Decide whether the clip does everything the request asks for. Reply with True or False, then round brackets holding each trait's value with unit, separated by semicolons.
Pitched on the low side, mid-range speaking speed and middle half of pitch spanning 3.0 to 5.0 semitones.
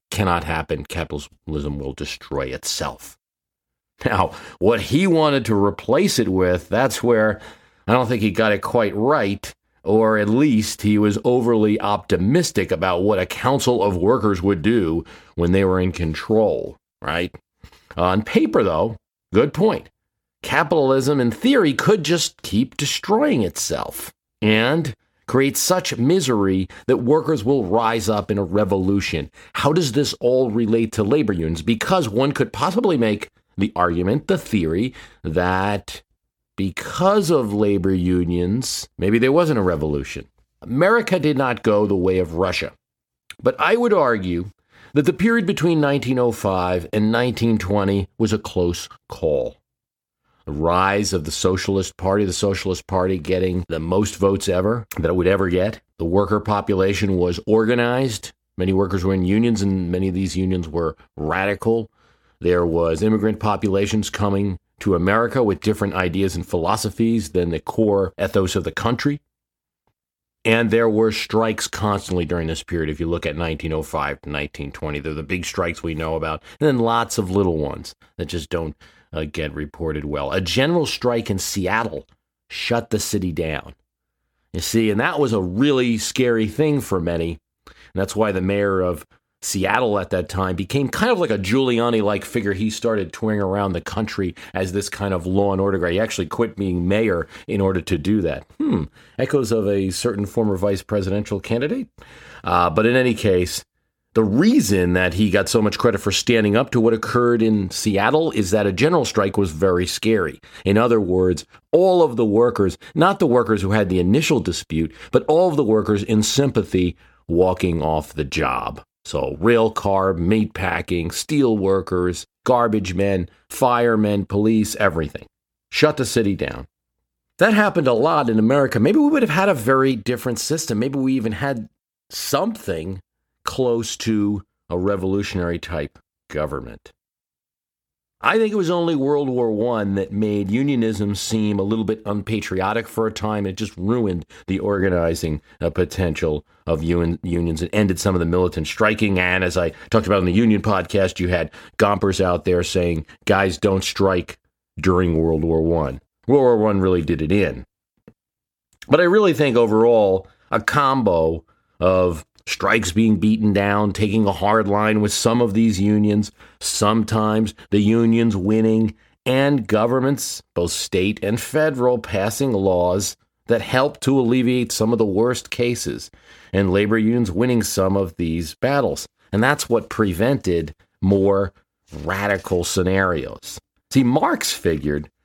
True (100 Hz; 165 wpm; 4.1 semitones)